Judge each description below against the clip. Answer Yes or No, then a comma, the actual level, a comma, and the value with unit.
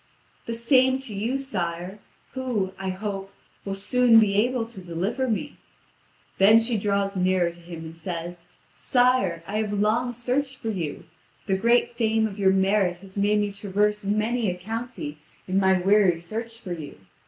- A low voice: No, high, 205 Hz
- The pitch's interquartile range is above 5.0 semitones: No, average, 3.6 semitones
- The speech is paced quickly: No, average, 170 wpm